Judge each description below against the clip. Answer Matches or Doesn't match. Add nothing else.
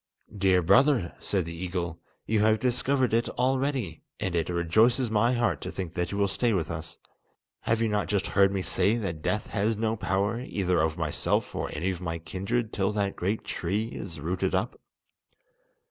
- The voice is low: Matches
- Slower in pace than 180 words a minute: Doesn't match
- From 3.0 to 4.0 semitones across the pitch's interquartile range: Doesn't match